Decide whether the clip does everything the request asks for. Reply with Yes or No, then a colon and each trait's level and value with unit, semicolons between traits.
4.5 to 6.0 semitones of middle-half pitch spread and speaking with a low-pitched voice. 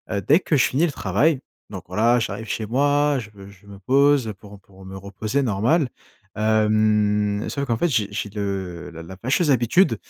Yes: wide, 5.4 semitones; low, 110 Hz